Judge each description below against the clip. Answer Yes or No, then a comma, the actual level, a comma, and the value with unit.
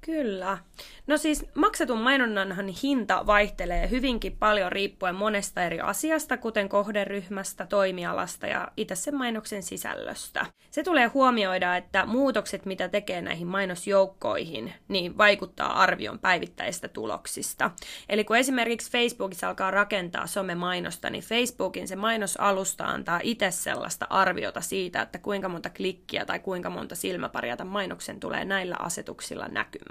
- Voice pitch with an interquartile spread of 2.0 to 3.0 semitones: No, average, 3.6 semitones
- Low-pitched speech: No, high, 200 Hz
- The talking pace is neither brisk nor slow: Yes, average, 130 wpm